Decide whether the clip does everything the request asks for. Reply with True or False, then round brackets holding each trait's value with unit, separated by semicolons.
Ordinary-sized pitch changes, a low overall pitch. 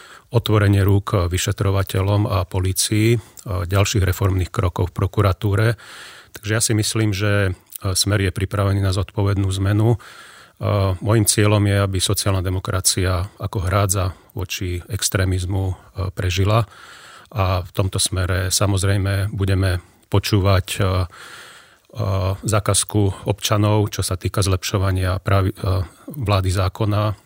False (1.8 semitones; 100 Hz)